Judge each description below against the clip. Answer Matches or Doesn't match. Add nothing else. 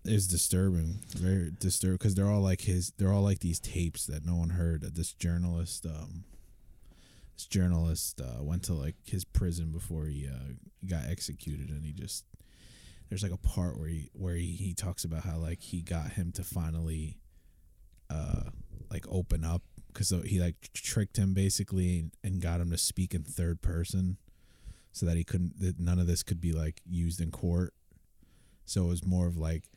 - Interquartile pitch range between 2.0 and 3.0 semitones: Matches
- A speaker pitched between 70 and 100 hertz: Matches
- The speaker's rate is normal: Matches